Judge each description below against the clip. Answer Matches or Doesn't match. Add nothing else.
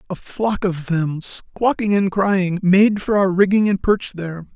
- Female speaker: Doesn't match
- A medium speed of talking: Matches